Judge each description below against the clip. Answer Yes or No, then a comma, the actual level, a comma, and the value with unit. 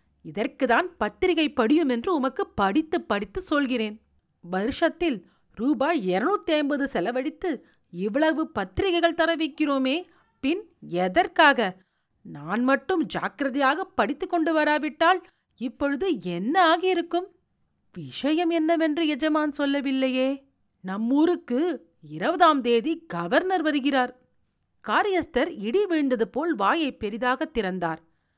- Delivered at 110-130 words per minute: No, average, 90 wpm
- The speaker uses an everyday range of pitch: No, wide, 6.0 semitones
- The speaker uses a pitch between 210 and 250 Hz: No, very high, 285 Hz